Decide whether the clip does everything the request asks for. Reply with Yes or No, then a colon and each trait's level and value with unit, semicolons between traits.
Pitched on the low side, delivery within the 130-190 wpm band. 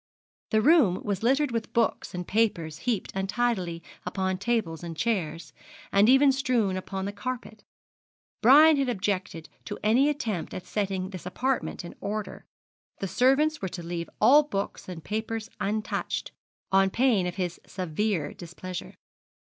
No: high, 205 Hz; average, 150 wpm